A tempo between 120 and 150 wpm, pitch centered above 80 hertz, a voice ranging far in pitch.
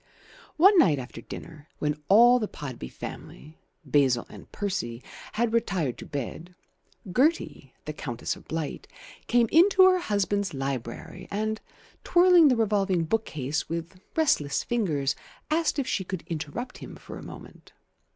Yes: average, 140 wpm; medium, 185 Hz; wide, 8.5 semitones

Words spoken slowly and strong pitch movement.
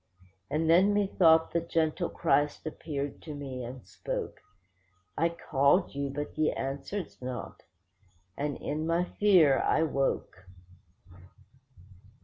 No: slow, 115 wpm; average, 3.7 semitones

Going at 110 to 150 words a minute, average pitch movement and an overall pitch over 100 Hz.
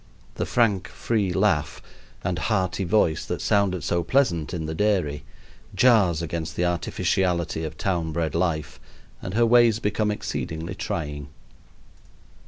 No: slow, 135 wpm; average, 4.3 semitones; very low, 90 Hz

